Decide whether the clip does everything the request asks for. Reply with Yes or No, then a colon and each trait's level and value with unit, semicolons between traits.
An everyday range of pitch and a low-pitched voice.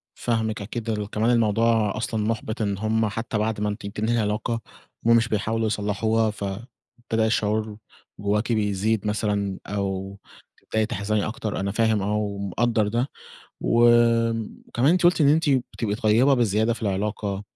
No: narrow, 1.9 semitones; low, 110 Hz